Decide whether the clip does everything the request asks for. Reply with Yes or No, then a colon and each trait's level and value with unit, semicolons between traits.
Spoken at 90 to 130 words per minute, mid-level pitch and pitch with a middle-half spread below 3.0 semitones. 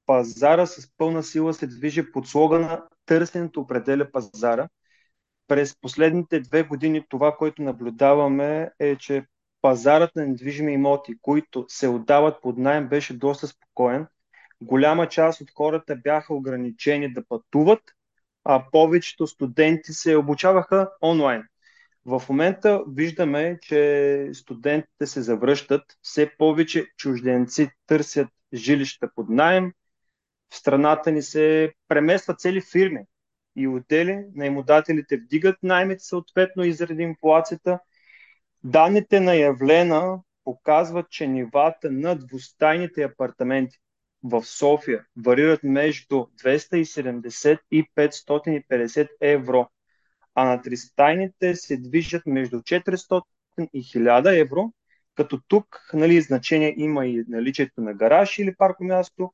No: slow, 115 wpm; medium, 150 Hz; average, 3.4 semitones